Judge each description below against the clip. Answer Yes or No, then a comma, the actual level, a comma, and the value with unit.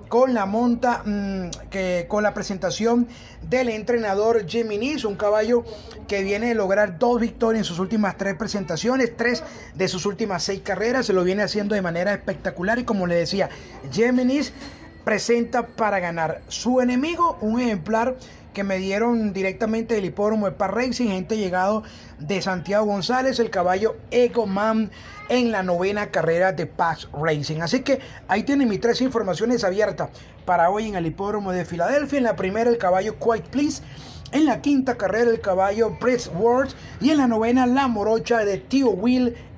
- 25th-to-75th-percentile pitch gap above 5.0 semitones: No, average, 3.8 semitones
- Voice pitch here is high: Yes, high, 215 Hz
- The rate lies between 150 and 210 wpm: Yes, average, 170 wpm